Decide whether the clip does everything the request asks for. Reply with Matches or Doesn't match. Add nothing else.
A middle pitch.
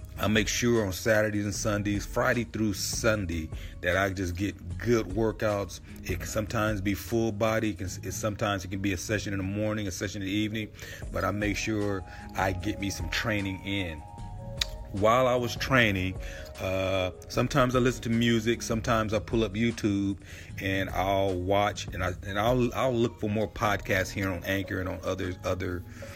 Doesn't match